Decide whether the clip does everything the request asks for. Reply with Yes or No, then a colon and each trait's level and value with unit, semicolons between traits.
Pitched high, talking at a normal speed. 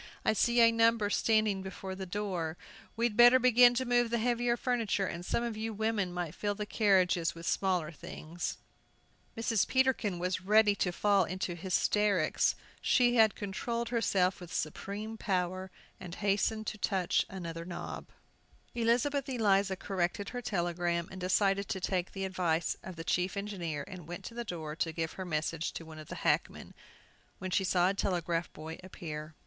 Yes: high, 195 Hz; average, 175 wpm